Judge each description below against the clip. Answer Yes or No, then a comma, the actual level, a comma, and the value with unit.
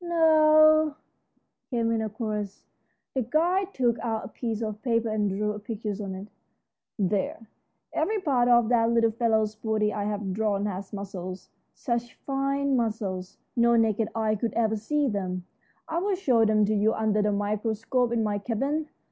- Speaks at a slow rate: No, average, 165 wpm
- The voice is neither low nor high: No, high, 225 Hz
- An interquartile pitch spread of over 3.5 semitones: No, average, 3.1 semitones